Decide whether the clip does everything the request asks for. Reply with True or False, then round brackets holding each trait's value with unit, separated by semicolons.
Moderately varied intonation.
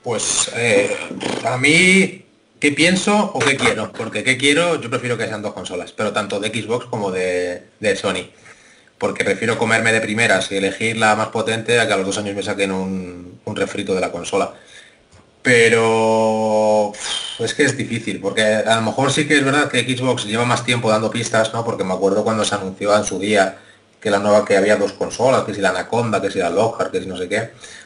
True (3.1 semitones)